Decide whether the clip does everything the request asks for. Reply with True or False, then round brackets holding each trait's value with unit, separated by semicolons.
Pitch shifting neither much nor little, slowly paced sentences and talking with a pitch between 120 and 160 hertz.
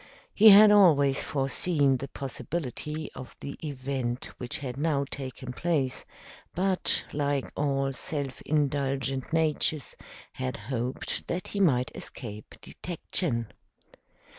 True (3.3 semitones; 115 wpm; 140 Hz)